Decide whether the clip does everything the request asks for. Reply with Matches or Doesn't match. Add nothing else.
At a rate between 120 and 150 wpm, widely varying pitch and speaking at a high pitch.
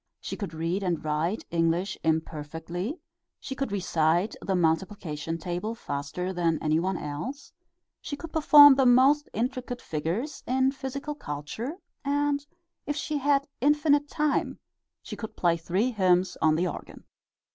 Matches